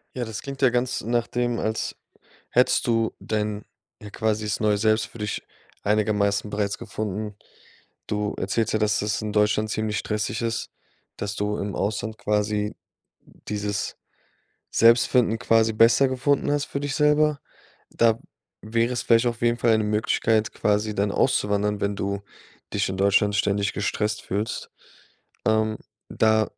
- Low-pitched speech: Yes, low, 110 Hz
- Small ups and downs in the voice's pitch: Yes, narrow, 1.9 semitones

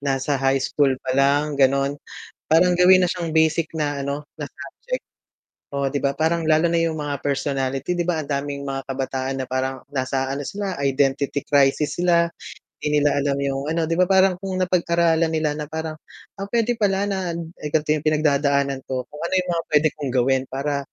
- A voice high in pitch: No, medium, 150 Hz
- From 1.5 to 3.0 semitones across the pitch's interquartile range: No, average, 3.5 semitones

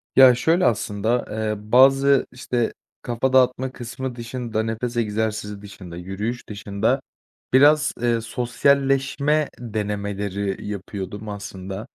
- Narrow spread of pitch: No, average, 4.1 semitones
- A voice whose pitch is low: Yes, low, 115 Hz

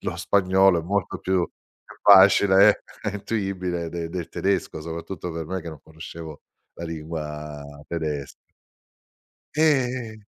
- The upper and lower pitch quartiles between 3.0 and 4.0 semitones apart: Yes, average, 3.4 semitones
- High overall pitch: No, very low, 90 Hz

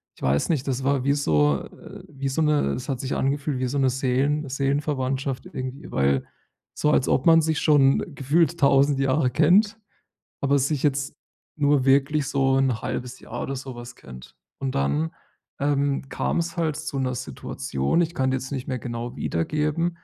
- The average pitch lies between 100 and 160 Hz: Yes, low, 135 Hz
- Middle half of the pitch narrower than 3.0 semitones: Yes, narrow, 2.6 semitones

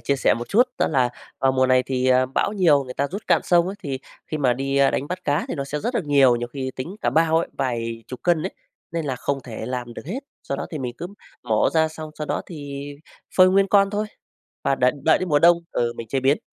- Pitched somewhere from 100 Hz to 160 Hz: Yes, medium, 140 Hz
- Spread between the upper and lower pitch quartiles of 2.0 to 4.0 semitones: No, average, 4.6 semitones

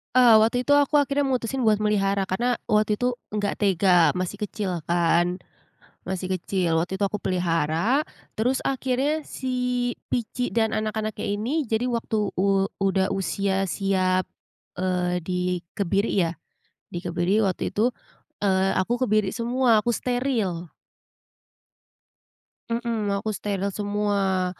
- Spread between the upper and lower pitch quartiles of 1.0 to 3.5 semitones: No, average, 4.2 semitones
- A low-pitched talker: No, high, 205 Hz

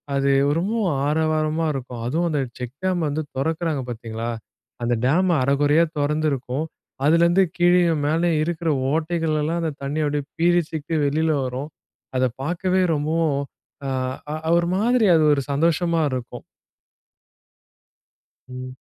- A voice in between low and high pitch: Yes, medium, 155 Hz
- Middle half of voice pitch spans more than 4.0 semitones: No, average, 3.3 semitones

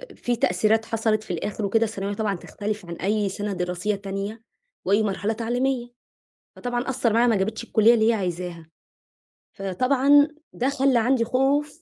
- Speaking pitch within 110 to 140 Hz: No, high, 220 Hz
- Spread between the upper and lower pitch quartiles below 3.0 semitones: No, average, 3.5 semitones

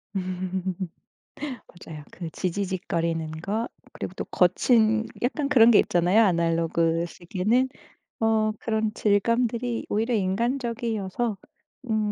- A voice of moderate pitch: No, high, 210 Hz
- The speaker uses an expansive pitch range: No, average, 4.3 semitones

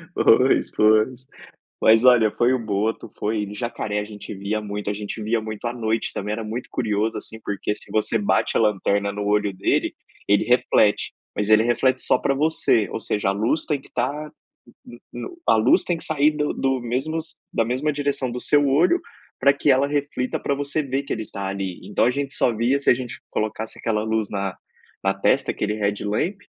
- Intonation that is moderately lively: Yes, average, 4.6 semitones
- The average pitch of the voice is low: Yes, low, 115 Hz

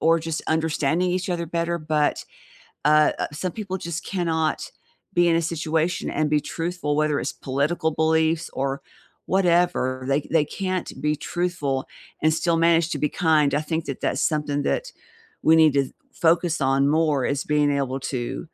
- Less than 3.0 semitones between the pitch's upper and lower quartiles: Yes, narrow, 2.5 semitones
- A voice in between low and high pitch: Yes, medium, 160 Hz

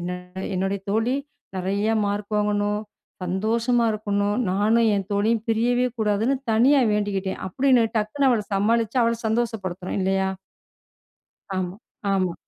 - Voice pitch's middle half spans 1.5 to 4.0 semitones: Yes, average, 2.8 semitones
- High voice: Yes, high, 210 Hz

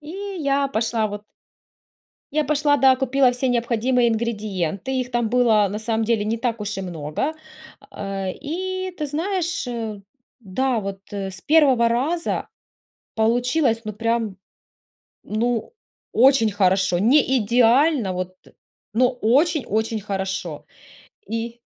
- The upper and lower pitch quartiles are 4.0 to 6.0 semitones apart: Yes, average, 4.3 semitones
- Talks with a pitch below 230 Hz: No, high, 235 Hz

